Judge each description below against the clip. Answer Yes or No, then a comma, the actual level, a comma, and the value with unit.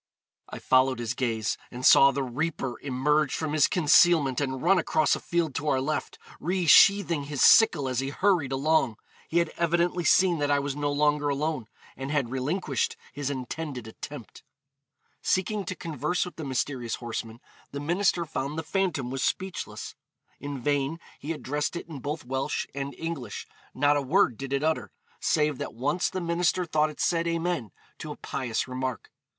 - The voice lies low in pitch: No, medium, 145 Hz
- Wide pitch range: No, average, 3.9 semitones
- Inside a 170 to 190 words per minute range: Yes, average, 175 wpm